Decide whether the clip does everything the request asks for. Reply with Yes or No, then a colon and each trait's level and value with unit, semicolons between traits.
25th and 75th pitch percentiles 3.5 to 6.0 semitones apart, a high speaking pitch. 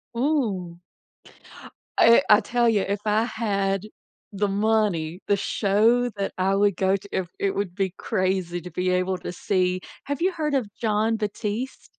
No: average, 3.1 semitones; high, 200 Hz